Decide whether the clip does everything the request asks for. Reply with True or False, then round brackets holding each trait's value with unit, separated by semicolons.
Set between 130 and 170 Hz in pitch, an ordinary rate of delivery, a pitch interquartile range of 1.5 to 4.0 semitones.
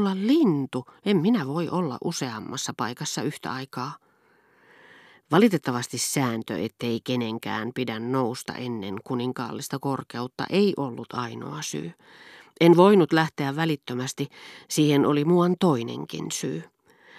False (140 Hz; 110 wpm; 5.6 semitones)